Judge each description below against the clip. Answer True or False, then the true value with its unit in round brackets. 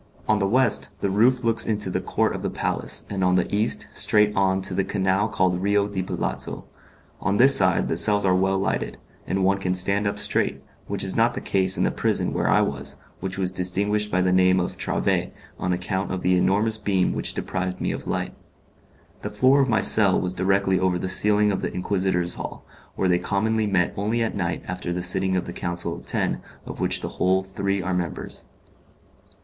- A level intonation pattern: True (2.0 semitones)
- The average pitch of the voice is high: False (95 Hz)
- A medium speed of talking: False (215 wpm)